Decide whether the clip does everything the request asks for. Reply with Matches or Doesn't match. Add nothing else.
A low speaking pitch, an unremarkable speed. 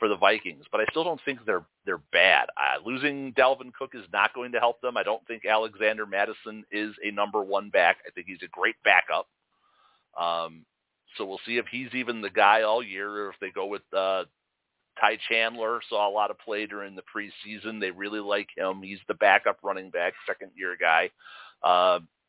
Doesn't match